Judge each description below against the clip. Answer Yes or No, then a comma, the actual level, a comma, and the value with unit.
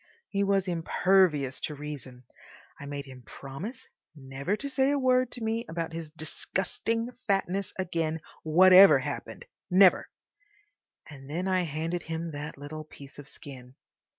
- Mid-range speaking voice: Yes, medium, 165 Hz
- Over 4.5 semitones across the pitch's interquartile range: Yes, average, 5.1 semitones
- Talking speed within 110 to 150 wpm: Yes, average, 140 wpm